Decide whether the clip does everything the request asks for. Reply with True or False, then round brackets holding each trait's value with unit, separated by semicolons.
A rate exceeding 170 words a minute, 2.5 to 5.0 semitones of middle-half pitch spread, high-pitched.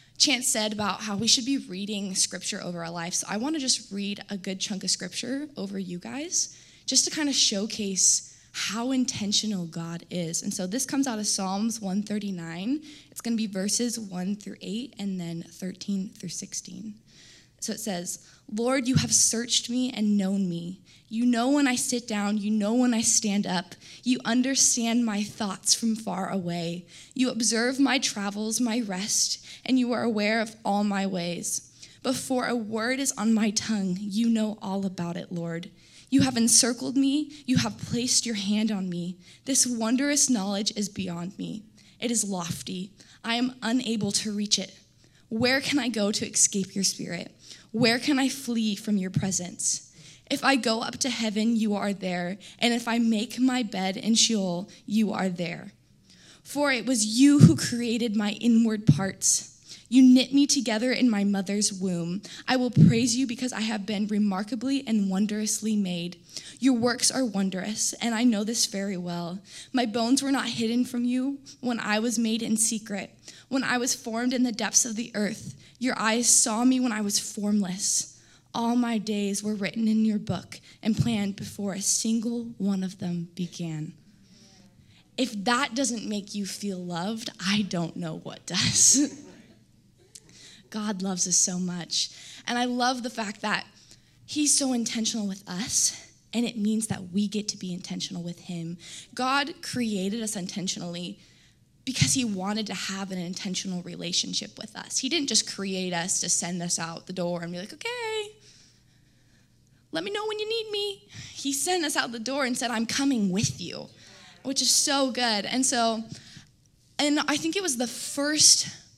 True (180 wpm; 4.4 semitones; 215 Hz)